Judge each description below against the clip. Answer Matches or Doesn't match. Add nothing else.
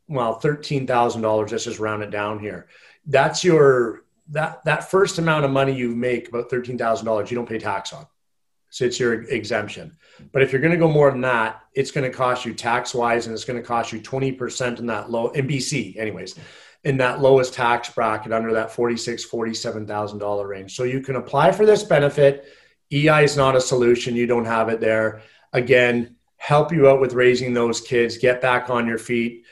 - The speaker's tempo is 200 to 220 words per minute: Matches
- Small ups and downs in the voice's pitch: Doesn't match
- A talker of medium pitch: Doesn't match